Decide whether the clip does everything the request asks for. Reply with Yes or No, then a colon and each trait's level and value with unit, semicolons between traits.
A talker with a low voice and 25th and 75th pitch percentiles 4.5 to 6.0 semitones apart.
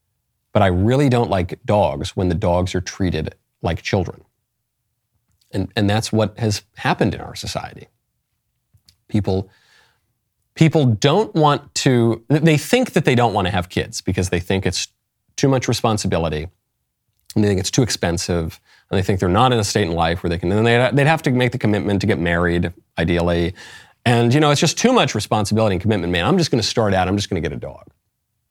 Yes: low, 105 Hz; average, 4.9 semitones